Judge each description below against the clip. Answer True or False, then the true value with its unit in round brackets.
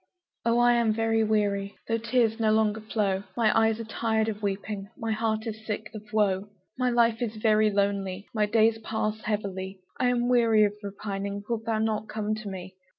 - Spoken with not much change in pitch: True (1.7 semitones)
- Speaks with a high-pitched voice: True (215 Hz)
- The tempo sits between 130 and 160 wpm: False (190 wpm)